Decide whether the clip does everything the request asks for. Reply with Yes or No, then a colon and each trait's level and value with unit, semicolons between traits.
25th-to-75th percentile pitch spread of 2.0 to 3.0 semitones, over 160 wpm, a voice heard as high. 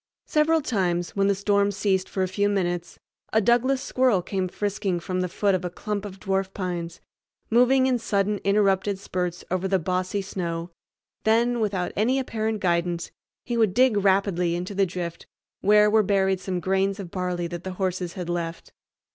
Yes: narrow, 2.6 semitones; average, 180 wpm; high, 195 Hz